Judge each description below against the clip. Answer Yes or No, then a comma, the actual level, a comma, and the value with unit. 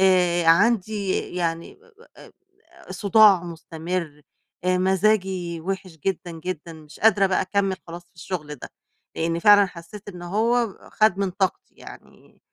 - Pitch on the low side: No, medium, 185 Hz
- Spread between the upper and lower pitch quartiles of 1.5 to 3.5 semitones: Yes, average, 2.8 semitones